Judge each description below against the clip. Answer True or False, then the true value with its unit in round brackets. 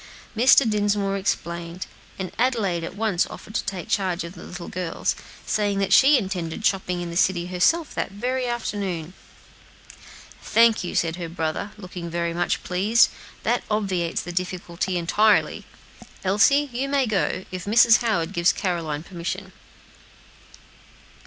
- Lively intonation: False (3.8 semitones)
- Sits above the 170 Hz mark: True (190 Hz)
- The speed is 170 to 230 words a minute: False (150 wpm)